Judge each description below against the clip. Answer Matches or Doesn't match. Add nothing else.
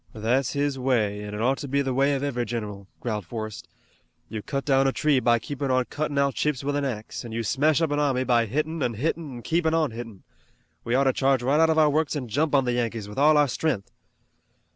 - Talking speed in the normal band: Doesn't match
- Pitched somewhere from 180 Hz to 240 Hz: Doesn't match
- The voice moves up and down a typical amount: Matches